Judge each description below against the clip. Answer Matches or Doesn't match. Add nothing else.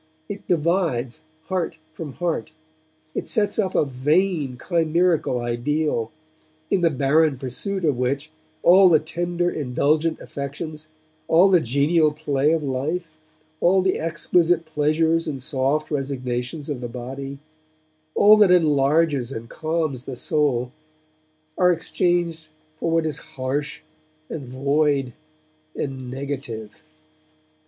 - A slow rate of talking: Matches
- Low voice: Doesn't match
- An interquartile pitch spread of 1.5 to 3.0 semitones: Doesn't match